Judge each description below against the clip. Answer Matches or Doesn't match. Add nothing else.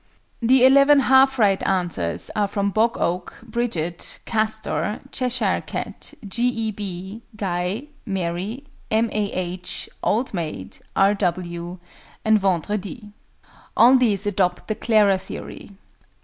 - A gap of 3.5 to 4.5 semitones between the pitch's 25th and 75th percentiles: Matches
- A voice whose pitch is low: Doesn't match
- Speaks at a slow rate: Matches